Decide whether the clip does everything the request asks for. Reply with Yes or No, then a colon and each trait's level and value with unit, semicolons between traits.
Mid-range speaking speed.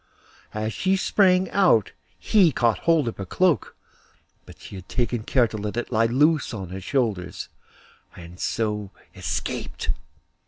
Yes: average, 150 wpm